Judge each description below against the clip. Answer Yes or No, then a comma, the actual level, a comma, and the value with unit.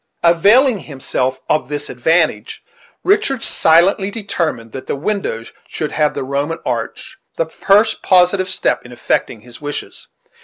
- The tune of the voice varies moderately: No, wide, 7.0 semitones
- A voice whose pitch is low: No, medium, 160 Hz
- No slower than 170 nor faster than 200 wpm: No, average, 140 wpm